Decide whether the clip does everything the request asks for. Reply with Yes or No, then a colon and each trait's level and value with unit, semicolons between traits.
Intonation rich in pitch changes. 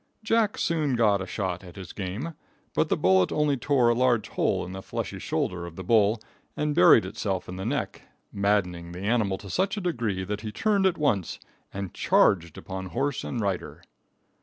Yes: wide, 6.9 semitones